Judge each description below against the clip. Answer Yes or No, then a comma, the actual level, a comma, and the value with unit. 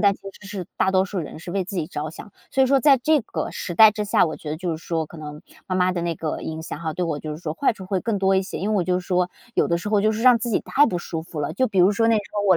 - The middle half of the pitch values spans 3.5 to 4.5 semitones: Yes, average, 4.1 semitones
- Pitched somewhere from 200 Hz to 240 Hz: No, medium, 185 Hz